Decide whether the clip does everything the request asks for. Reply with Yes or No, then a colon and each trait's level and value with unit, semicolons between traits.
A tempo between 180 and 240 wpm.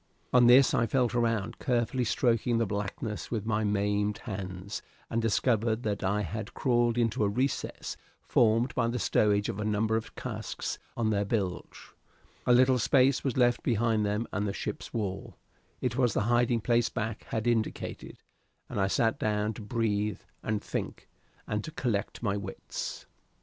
No: average, 170 wpm